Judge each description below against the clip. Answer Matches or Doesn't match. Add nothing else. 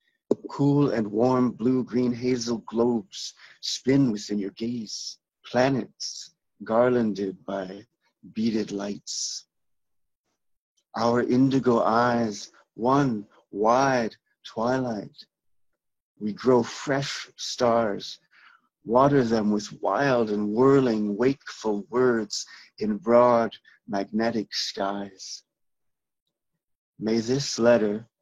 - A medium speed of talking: Doesn't match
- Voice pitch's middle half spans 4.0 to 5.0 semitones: Doesn't match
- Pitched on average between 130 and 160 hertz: Doesn't match